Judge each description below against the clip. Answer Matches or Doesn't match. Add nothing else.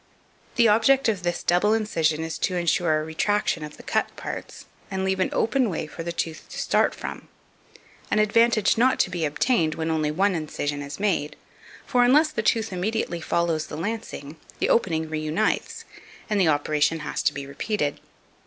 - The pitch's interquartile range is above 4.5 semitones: Matches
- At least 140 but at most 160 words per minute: Doesn't match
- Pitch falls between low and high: Matches